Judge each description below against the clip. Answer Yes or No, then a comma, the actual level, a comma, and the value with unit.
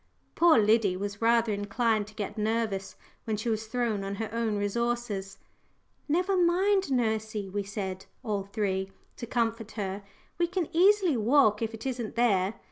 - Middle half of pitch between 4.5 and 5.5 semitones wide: No, average, 3.0 semitones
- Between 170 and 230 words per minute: No, average, 160 wpm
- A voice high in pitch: Yes, high, 220 Hz